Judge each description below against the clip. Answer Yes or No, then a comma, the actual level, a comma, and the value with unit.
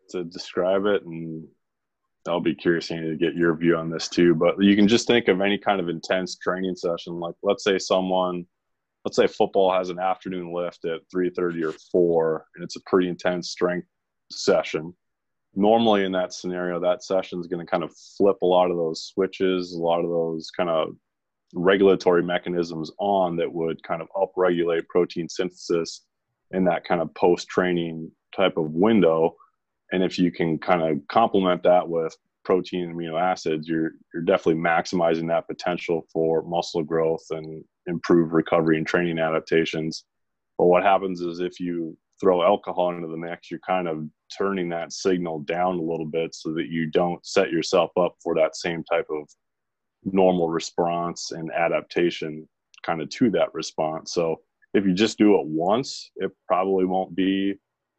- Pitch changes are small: Yes, narrow, 2.0 semitones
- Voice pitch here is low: Yes, very low, 85 Hz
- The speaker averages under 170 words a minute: No, average, 175 wpm